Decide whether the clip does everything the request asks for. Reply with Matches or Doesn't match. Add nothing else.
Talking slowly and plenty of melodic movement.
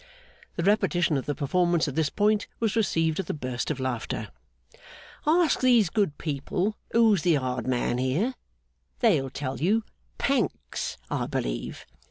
Doesn't match